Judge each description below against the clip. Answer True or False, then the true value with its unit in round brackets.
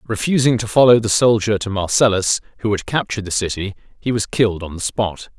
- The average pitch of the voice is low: True (105 Hz)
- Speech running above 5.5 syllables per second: True (5.9 syllables/s)